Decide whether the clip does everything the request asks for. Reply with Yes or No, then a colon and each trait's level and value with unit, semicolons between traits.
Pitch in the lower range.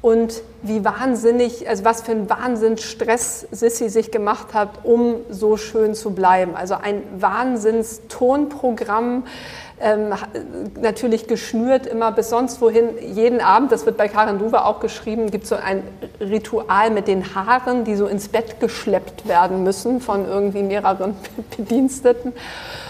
No: high, 225 Hz